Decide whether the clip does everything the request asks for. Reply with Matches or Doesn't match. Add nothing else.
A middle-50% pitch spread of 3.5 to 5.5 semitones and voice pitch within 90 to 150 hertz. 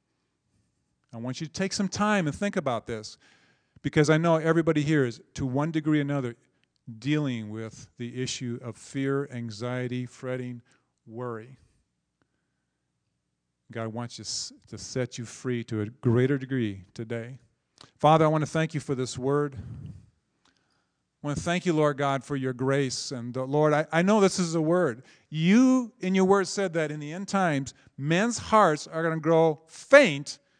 Matches